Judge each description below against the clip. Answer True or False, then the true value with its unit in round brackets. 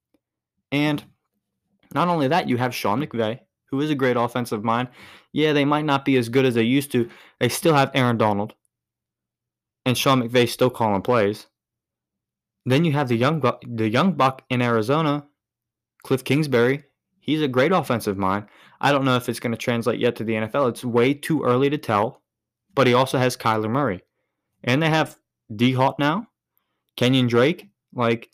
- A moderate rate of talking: True (185 wpm)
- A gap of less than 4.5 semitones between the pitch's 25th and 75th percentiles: True (3.3 semitones)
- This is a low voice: True (125 Hz)